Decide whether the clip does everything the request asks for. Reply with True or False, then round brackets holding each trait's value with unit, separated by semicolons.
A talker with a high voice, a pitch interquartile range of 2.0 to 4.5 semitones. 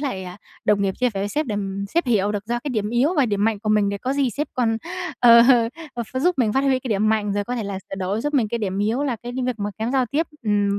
True (225 Hz; 3.8 semitones)